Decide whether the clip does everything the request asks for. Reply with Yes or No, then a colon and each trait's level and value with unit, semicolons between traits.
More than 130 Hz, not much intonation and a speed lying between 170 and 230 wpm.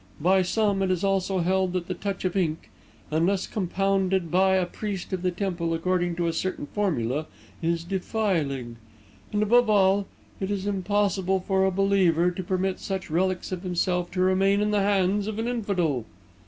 Yes: high, 190 Hz; narrow, 2.0 semitones; average, 180 wpm